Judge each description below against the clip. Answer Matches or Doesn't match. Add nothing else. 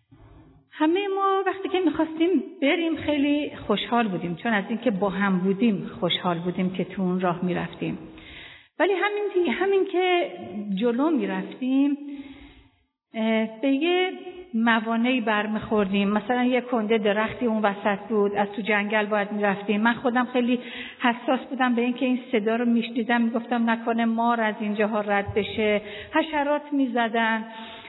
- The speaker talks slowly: Doesn't match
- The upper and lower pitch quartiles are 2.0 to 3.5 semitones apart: Doesn't match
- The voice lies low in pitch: Doesn't match